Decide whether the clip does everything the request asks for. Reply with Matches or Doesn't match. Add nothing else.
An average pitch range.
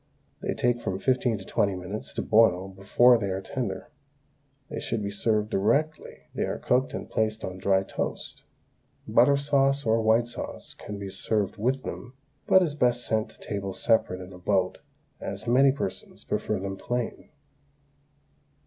Matches